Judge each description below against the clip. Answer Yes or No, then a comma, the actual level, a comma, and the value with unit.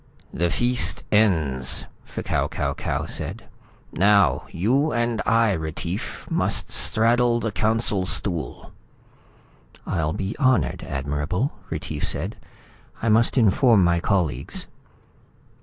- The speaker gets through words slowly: Yes, slow, 110 wpm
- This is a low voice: Yes, low, 100 Hz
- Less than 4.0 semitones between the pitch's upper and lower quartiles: No, wide, 5.6 semitones